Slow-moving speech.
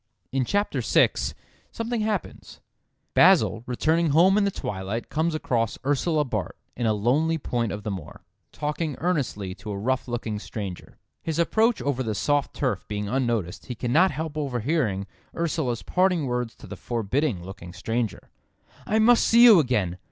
No: average, 160 wpm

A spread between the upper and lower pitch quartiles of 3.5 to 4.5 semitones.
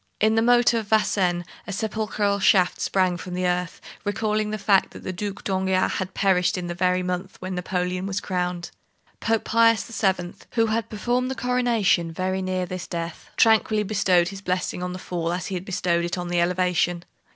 No: average, 3.0 semitones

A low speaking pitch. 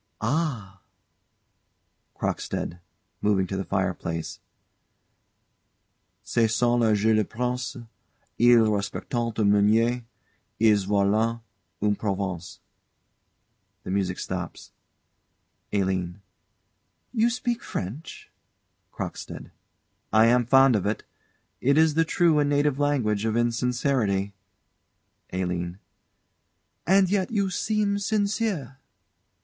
Yes: low, 115 Hz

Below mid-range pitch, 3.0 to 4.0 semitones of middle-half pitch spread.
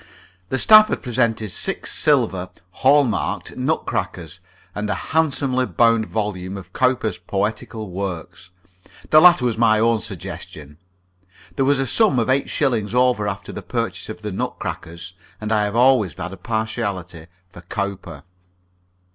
No: low, 110 Hz; average, 4.7 semitones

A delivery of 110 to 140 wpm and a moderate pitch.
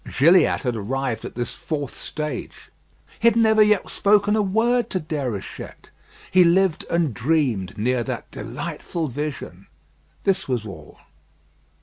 Yes: slow, 135 wpm; medium, 155 Hz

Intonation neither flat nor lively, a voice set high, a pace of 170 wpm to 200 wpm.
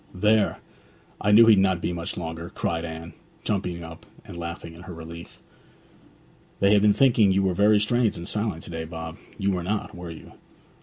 No: average, 3.7 semitones; very low, 90 Hz; average, 195 wpm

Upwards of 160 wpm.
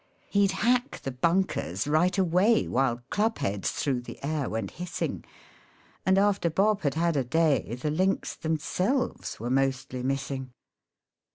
No: average, 145 wpm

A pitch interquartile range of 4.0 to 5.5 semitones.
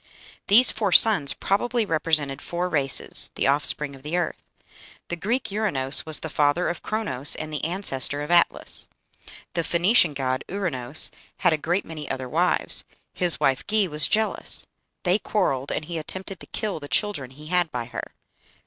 Yes: average, 5.1 semitones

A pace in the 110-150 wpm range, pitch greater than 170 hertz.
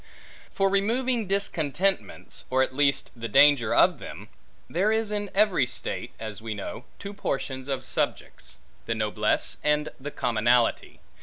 No: average, 145 wpm; medium, 145 Hz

